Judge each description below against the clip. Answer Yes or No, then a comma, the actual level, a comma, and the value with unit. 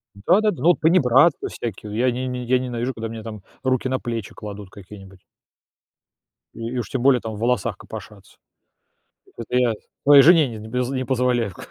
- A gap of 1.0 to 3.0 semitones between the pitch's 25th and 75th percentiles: Yes, average, 2.7 semitones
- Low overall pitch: Yes, low, 125 Hz